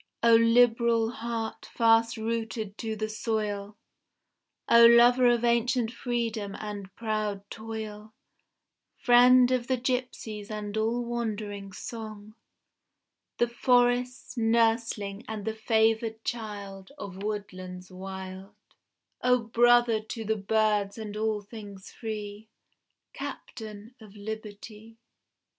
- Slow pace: Yes, slow, 110 wpm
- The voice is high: Yes, high, 220 Hz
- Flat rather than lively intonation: Yes, narrow, 2.1 semitones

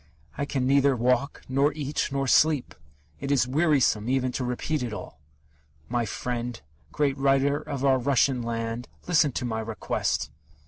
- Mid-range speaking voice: No, low, 130 Hz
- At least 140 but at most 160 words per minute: Yes, average, 155 wpm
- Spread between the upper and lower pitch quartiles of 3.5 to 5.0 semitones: No, narrow, 2.5 semitones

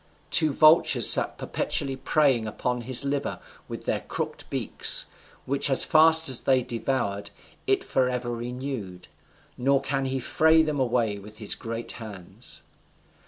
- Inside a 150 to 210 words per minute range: No, average, 140 wpm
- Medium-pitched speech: No, low, 130 Hz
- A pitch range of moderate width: Yes, average, 3.2 semitones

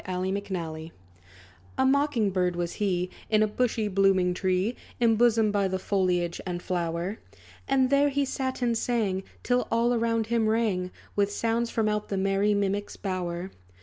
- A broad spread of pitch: No, average, 4.0 semitones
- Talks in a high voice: Yes, high, 205 Hz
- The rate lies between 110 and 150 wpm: No, average, 165 wpm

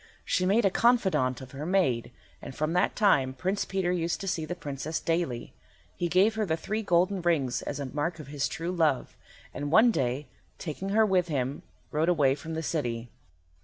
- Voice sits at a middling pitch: Yes, medium, 165 Hz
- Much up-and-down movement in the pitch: No, average, 4.8 semitones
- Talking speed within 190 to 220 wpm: Yes, average, 200 wpm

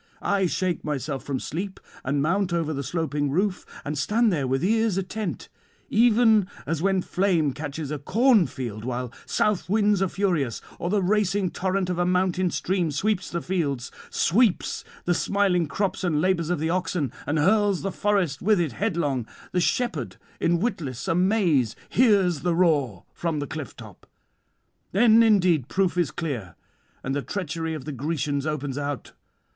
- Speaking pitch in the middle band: Yes, medium, 175 Hz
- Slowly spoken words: No, average, 165 wpm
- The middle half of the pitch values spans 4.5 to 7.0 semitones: Yes, average, 5.1 semitones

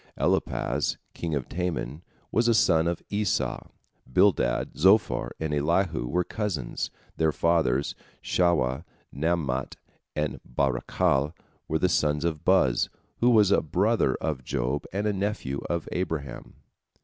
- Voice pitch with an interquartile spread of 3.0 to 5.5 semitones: Yes, average, 5.0 semitones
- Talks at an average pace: No, slow, 130 wpm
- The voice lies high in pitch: No, very low, 80 Hz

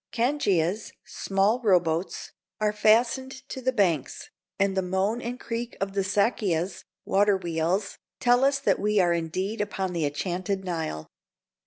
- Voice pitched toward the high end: Yes, high, 195 Hz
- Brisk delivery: No, average, 145 wpm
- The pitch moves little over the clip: No, average, 4.3 semitones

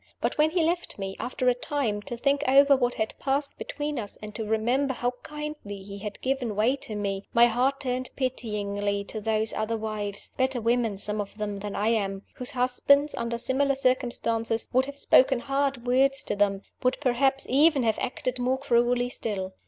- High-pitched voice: Yes, high, 245 Hz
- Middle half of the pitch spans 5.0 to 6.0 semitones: No, average, 4.1 semitones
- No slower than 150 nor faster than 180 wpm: No, average, 190 wpm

